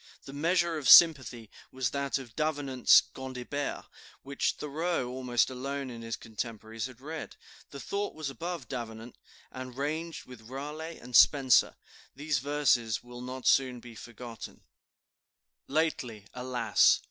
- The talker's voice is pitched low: Yes, low, 130 Hz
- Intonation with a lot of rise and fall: No, average, 3.3 semitones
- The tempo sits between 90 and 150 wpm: Yes, slow, 135 wpm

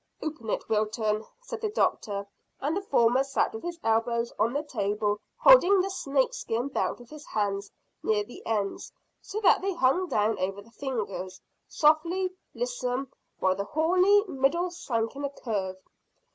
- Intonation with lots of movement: Yes, wide, 8.1 semitones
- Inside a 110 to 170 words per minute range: Yes, average, 160 wpm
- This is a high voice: Yes, very high, 255 Hz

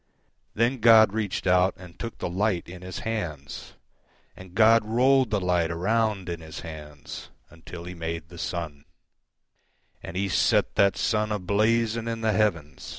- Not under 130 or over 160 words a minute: Yes, average, 150 wpm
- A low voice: Yes, very low, 95 Hz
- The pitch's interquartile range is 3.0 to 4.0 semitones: No, average, 4.6 semitones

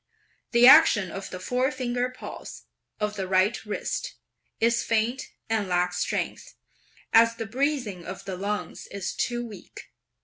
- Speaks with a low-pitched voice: No, high, 220 Hz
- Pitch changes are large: No, average, 4.1 semitones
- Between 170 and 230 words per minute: No, average, 140 wpm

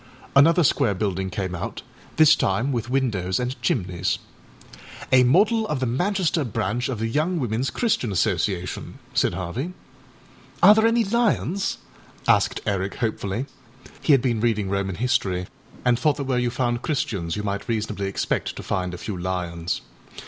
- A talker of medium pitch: No, low, 120 Hz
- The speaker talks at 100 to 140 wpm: No, average, 160 wpm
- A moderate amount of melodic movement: No, wide, 6.6 semitones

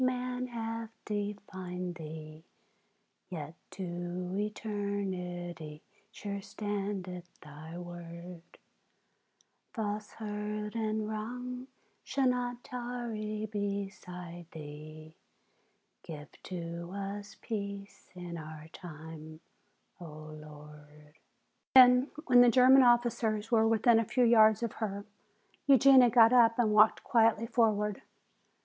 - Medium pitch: No, high, 205 Hz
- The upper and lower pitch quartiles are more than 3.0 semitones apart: Yes, average, 4.7 semitones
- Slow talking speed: Yes, slow, 100 wpm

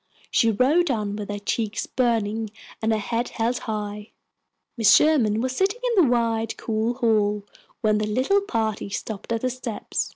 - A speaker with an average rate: Yes, average, 170 wpm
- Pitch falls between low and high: No, high, 225 Hz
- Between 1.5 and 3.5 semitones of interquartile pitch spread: Yes, average, 3.0 semitones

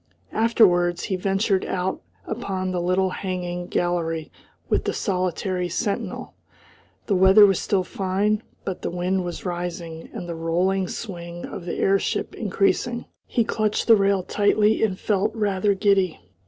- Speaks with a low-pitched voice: No, high, 190 Hz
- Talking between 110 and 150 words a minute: Yes, average, 145 wpm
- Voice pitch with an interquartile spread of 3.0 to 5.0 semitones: No, narrow, 2.4 semitones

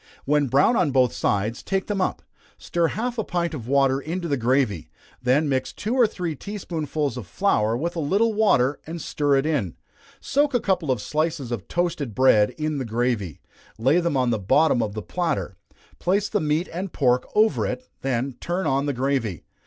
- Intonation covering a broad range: Yes, wide, 5.9 semitones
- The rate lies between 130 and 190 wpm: No, average, 200 wpm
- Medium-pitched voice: Yes, medium, 145 Hz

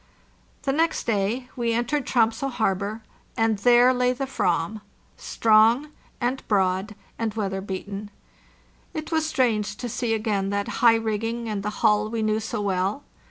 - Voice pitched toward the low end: No, high, 220 Hz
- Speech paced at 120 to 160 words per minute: Yes, average, 155 wpm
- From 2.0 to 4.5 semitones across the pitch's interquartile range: Yes, average, 2.9 semitones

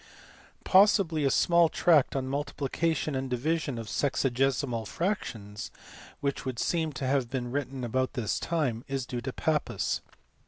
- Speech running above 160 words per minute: No, average, 145 wpm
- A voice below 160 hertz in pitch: Yes, low, 135 Hz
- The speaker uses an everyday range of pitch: Yes, average, 4.1 semitones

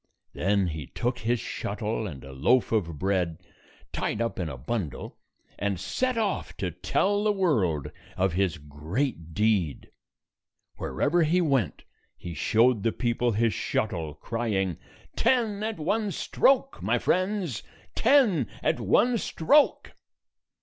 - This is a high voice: No, low, 110 Hz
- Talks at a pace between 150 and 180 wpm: No, slow, 135 wpm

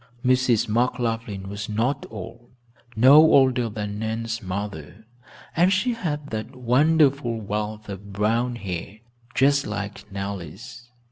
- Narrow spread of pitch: No, average, 3.7 semitones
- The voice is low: Yes, low, 115 Hz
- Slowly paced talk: Yes, slow, 120 wpm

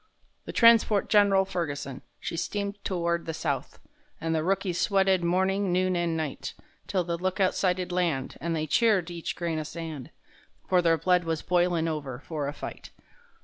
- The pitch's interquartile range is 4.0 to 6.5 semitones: No, narrow, 2.6 semitones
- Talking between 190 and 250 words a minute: No, average, 175 wpm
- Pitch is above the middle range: No, medium, 175 Hz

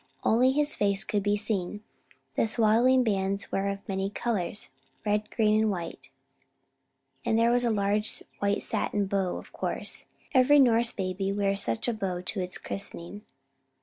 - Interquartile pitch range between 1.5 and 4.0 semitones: Yes, narrow, 2.6 semitones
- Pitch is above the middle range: Yes, high, 205 Hz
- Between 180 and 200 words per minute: No, average, 160 wpm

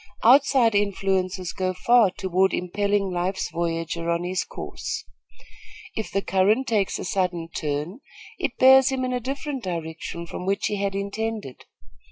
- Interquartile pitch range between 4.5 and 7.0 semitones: No, average, 4.1 semitones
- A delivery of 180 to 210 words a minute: No, average, 150 wpm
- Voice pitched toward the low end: No, high, 195 Hz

